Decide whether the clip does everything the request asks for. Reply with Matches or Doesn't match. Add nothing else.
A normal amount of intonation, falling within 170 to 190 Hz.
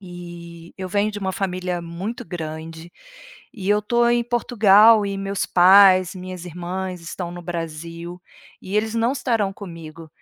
Matches